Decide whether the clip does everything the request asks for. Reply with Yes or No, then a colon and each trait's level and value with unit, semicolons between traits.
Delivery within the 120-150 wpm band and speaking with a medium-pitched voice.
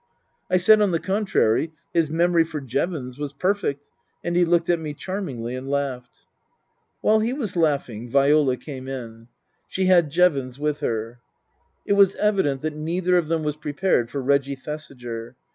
No: average, 165 wpm; medium, 150 Hz